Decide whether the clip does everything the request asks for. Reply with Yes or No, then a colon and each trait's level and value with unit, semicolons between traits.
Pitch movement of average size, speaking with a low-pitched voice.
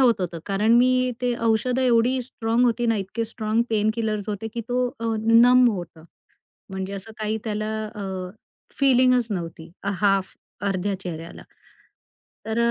No: average, 3.4 semitones; high, 220 Hz